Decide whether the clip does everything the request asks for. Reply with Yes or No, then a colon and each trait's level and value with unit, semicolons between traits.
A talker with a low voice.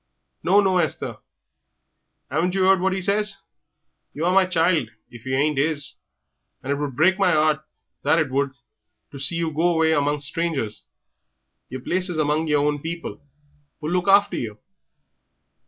No: medium, 160 Hz